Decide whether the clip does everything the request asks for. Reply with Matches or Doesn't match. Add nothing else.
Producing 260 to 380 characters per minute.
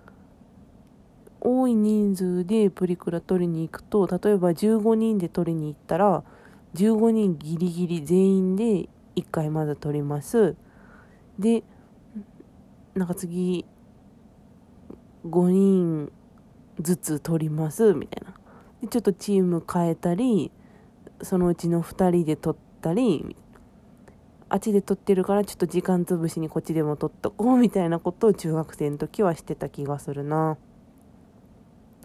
Doesn't match